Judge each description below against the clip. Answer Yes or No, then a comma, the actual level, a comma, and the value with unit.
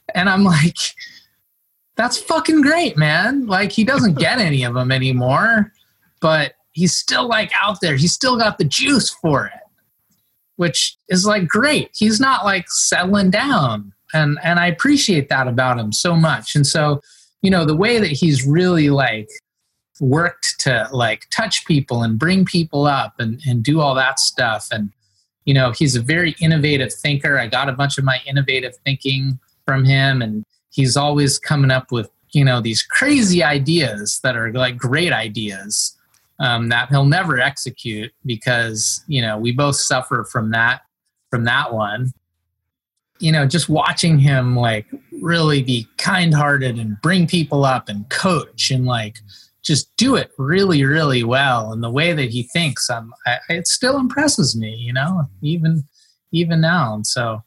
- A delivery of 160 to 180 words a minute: Yes, average, 170 wpm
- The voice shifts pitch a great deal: Yes, wide, 5.8 semitones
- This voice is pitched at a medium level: Yes, medium, 145 Hz